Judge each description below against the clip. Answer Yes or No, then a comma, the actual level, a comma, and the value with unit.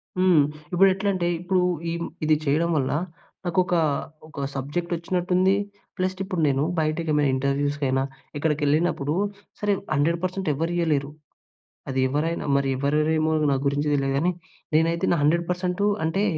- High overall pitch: No, medium, 160 Hz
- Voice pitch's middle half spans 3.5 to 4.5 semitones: Yes, average, 3.8 semitones